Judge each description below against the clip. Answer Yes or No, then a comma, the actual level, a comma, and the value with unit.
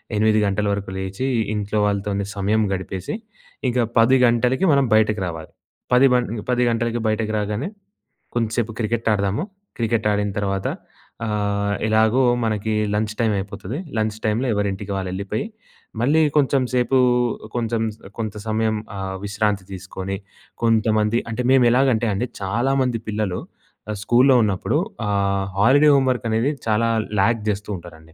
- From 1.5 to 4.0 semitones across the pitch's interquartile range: Yes, average, 2.8 semitones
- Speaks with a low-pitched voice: Yes, low, 110 Hz